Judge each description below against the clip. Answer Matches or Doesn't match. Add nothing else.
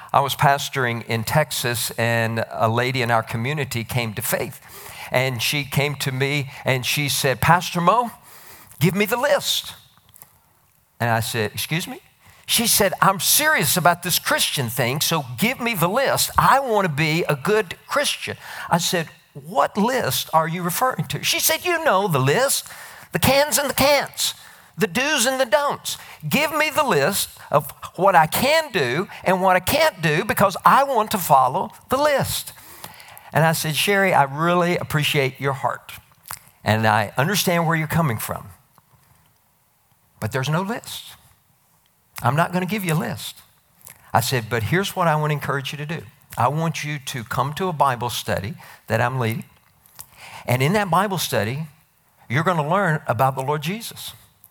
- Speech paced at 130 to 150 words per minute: Doesn't match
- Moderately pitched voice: Matches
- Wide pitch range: Matches